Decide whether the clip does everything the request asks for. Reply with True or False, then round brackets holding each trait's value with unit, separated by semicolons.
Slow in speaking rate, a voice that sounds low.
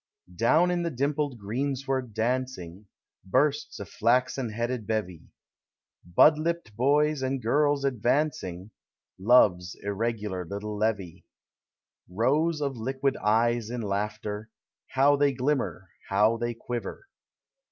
True (110 wpm; 120 Hz)